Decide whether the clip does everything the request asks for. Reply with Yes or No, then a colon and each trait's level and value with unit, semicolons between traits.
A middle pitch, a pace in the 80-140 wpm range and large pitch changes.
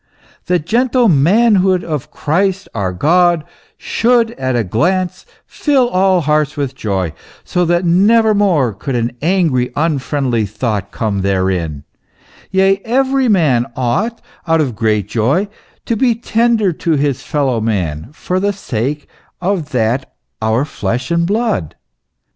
Yes: medium, 155 Hz; slow, 135 wpm; wide, 8.5 semitones